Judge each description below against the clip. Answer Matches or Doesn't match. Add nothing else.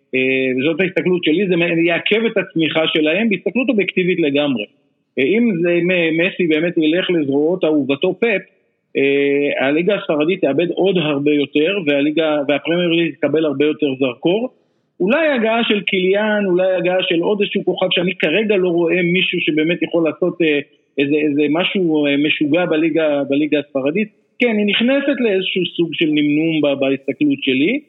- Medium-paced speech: Matches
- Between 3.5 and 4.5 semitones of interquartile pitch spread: Matches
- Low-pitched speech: Doesn't match